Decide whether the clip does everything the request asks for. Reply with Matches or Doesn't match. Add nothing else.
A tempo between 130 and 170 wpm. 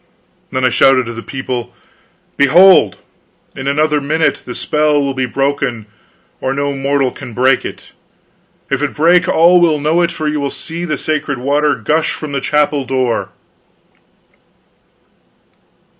Matches